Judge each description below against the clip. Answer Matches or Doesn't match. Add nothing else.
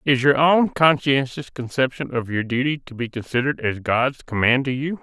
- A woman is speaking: Doesn't match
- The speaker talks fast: Doesn't match